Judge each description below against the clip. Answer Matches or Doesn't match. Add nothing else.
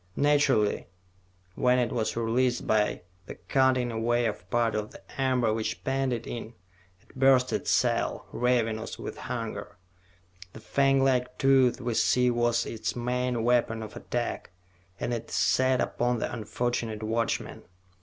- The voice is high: Doesn't match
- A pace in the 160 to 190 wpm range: Doesn't match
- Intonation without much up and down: Matches